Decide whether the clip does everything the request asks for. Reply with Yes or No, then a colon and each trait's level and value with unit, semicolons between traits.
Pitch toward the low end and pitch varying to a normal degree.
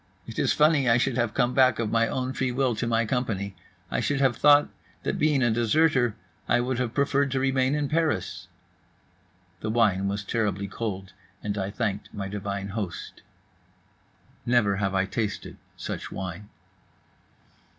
Yes: low, 115 Hz; average, 4.5 semitones